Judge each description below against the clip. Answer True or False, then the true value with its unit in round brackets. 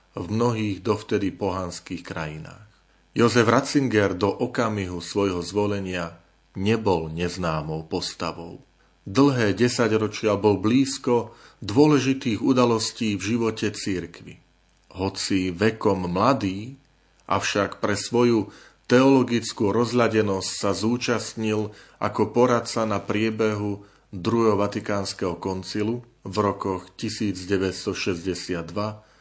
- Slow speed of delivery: True (90 wpm)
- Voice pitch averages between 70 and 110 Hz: True (105 Hz)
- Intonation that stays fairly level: False (3.4 semitones)